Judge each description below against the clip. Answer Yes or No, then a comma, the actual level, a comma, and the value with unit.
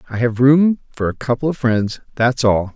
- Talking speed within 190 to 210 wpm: No, fast, 220 wpm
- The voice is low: Yes, low, 125 Hz